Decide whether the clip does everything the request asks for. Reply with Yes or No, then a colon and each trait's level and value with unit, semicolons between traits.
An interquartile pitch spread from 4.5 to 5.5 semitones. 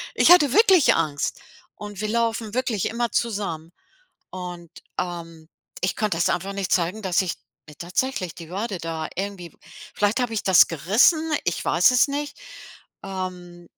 Yes: average, 5.1 semitones